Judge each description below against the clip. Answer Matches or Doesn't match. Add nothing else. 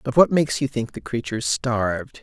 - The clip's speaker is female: Doesn't match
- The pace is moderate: Doesn't match